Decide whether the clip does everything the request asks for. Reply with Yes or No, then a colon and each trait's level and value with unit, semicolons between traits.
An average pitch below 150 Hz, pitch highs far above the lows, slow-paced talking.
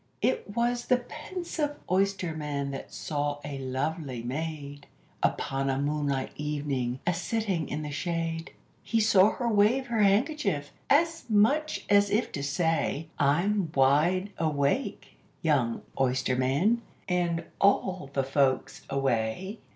No: medium, 160 Hz; wide, 6.6 semitones; slow, 125 wpm